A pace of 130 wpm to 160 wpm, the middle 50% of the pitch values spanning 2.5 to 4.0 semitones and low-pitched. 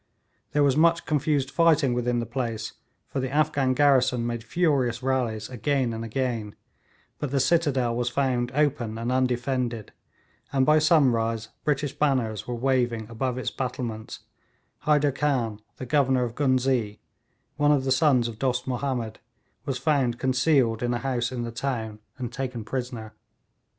Yes: average, 155 wpm; average, 2.8 semitones; low, 130 Hz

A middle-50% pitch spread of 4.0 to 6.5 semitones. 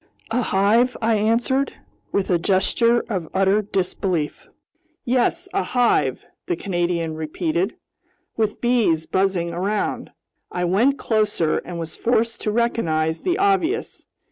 Yes: wide, 5.4 semitones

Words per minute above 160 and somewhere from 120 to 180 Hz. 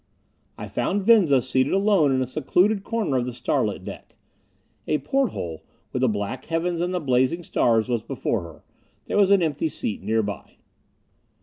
Yes: average, 170 wpm; medium, 140 Hz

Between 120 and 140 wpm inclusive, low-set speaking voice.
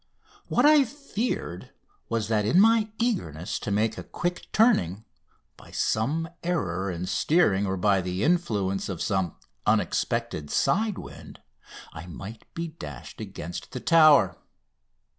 Yes: slow, 135 wpm; low, 110 Hz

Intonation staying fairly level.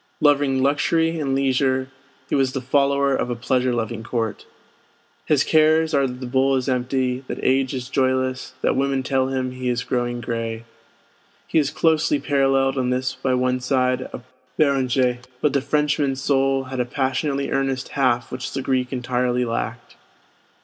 Yes: narrow, 1.5 semitones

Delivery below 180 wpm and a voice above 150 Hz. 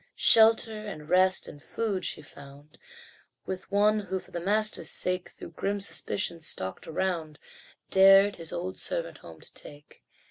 Yes: average, 150 wpm; high, 190 Hz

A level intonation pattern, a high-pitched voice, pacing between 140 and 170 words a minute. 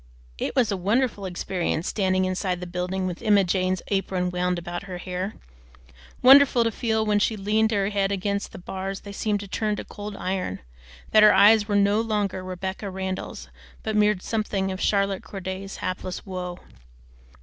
No: narrow, 2.1 semitones; high, 195 Hz; average, 180 wpm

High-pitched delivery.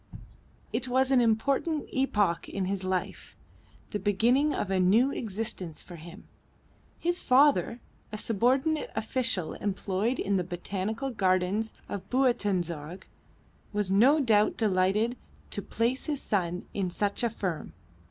Yes: high, 210 Hz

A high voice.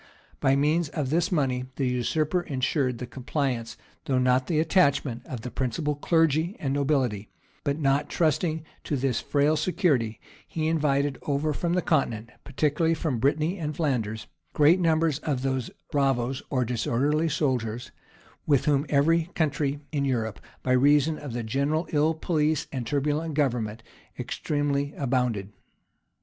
No: medium, 140 Hz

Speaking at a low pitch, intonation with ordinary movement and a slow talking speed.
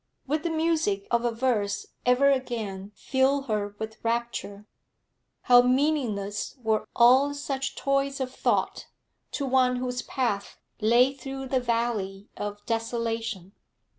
No: high, 245 Hz; average, 3.7 semitones; slow, 130 wpm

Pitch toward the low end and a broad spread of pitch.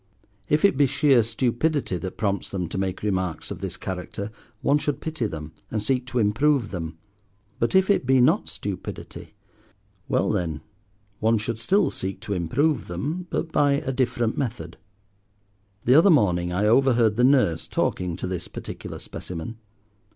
Yes: low, 115 Hz; wide, 6.8 semitones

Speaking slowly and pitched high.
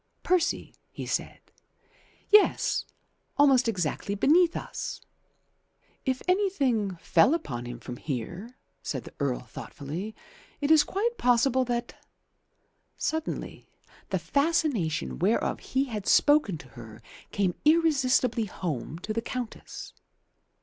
Yes: slow, 115 wpm; high, 235 Hz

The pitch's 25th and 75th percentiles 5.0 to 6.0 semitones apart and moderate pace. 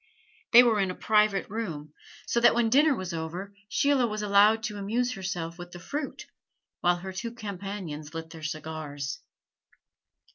Yes: average, 5.3 semitones; average, 160 wpm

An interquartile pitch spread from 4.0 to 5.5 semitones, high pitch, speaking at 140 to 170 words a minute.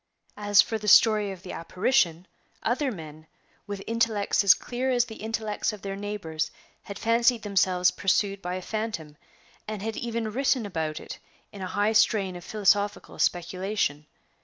No: average, 3.3 semitones; high, 205 Hz; average, 160 wpm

